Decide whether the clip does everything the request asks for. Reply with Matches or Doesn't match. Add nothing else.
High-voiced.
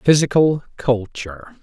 Doesn't match